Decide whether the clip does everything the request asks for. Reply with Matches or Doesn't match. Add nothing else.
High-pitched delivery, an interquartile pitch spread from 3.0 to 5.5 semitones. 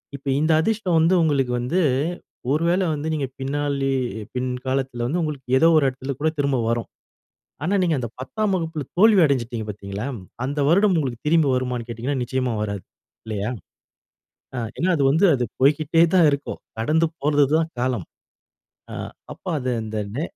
Doesn't match